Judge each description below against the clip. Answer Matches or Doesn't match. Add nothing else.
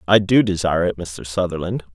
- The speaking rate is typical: Matches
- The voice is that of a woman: Doesn't match